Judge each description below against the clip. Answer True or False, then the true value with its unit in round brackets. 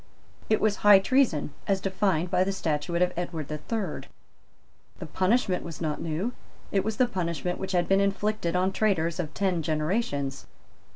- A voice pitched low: False (185 Hz)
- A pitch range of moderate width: True (3.4 semitones)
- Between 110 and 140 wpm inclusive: False (170 wpm)